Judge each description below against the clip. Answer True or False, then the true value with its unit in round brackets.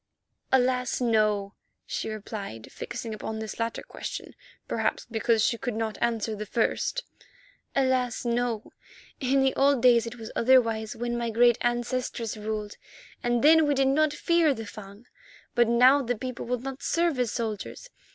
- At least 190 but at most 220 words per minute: False (160 wpm)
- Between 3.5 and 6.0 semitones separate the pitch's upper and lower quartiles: False (2.8 semitones)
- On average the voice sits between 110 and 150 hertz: False (240 Hz)